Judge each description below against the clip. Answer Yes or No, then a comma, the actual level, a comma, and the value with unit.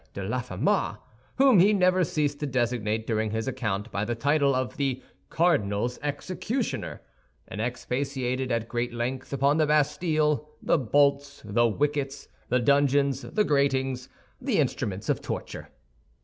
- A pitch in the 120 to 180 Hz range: Yes, low, 135 Hz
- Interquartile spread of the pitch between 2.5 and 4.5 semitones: Yes, average, 3.7 semitones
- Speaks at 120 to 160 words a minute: Yes, average, 140 wpm